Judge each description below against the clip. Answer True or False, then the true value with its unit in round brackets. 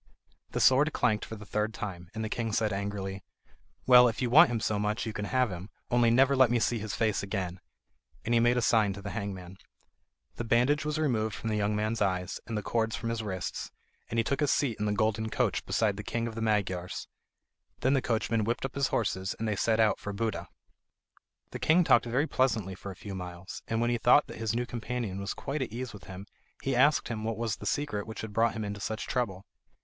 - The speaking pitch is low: True (110 Hz)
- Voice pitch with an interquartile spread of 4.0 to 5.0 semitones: False (2.8 semitones)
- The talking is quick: True (240 wpm)